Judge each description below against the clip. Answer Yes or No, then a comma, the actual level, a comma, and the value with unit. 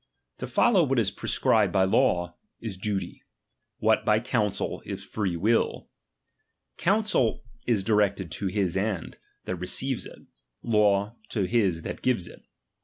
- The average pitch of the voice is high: No, low, 105 Hz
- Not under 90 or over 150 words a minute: Yes, average, 145 wpm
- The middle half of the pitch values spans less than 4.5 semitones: Yes, average, 3.6 semitones